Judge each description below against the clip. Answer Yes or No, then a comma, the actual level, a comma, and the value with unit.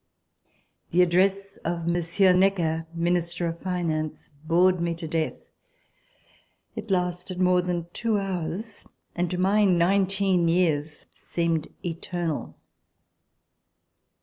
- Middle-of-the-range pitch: Yes, medium, 175 Hz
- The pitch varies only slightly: Yes, narrow, 1.9 semitones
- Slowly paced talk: Yes, slow, 105 wpm